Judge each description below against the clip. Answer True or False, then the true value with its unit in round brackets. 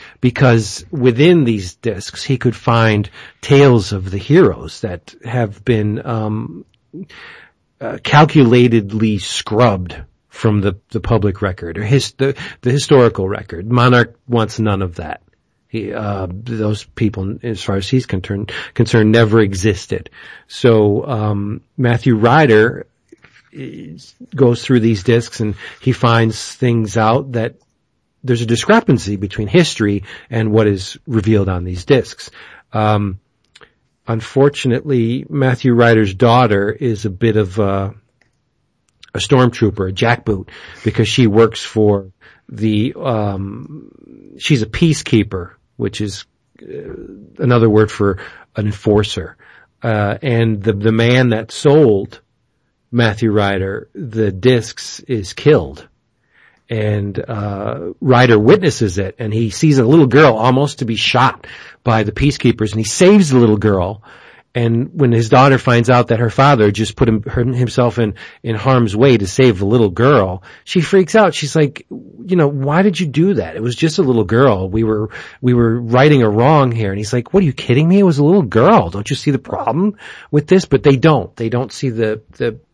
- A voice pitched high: False (115 Hz)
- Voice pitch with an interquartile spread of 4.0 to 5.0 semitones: False (3.5 semitones)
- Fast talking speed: False (155 wpm)